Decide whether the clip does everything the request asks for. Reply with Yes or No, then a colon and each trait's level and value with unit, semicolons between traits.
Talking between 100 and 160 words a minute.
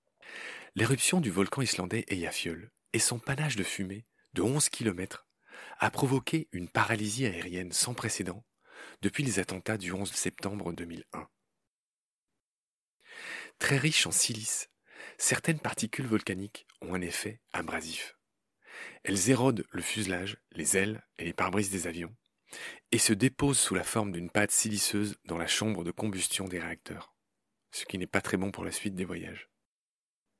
Yes: average, 150 wpm